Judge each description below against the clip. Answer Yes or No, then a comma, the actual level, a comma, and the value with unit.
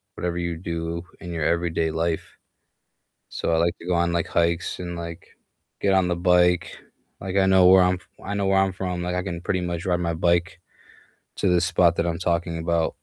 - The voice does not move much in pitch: Yes, narrow, 1.2 semitones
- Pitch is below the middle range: Yes, very low, 85 Hz